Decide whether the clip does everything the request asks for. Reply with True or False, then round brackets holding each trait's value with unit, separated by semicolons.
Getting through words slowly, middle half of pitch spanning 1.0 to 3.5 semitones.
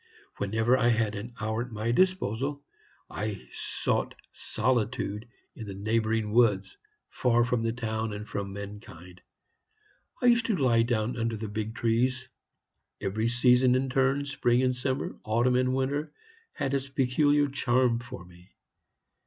False (145 wpm; 3.0 semitones)